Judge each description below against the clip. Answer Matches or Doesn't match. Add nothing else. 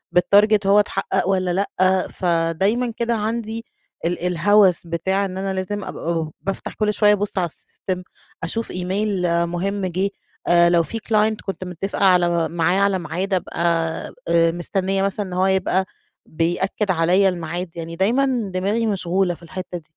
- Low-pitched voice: Doesn't match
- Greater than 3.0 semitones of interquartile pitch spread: Doesn't match